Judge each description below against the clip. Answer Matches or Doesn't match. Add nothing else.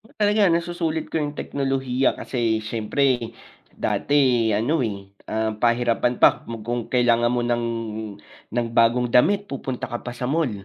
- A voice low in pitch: Matches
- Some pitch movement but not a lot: Matches